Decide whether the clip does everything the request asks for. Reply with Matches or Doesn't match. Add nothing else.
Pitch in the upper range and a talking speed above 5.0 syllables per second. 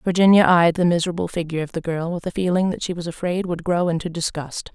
Doesn't match